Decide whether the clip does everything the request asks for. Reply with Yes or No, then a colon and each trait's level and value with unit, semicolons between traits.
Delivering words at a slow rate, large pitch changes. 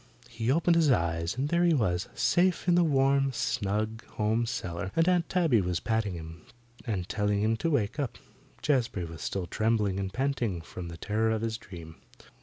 No: average, 190 wpm; wide, 6.5 semitones